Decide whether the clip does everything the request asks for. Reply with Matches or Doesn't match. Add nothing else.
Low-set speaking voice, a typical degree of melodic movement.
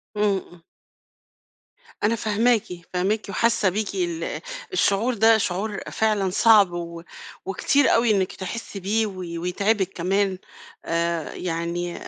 Doesn't match